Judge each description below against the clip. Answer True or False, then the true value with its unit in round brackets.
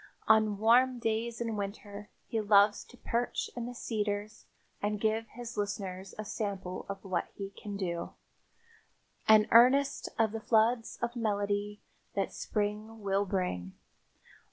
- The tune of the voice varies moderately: False (2.0 semitones)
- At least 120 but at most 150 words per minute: True (140 wpm)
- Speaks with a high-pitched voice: True (210 Hz)